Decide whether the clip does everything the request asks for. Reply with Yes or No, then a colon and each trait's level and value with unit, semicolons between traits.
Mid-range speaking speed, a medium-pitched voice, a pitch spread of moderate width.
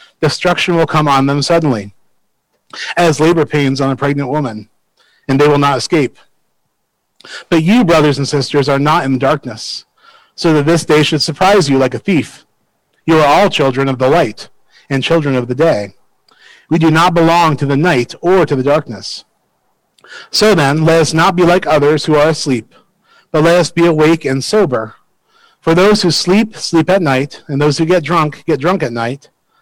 Yes: average, 190 wpm; medium, 155 Hz; average, 3.9 semitones